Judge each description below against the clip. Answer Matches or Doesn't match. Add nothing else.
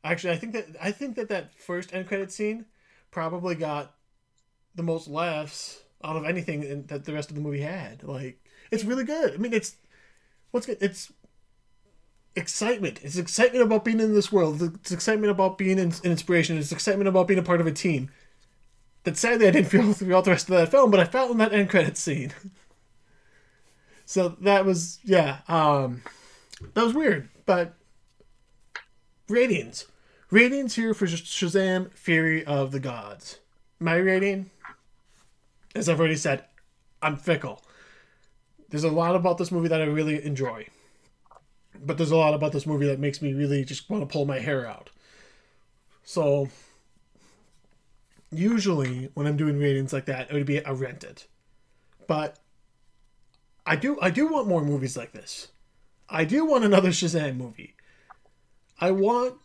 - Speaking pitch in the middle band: Matches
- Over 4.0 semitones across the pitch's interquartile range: Matches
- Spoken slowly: Doesn't match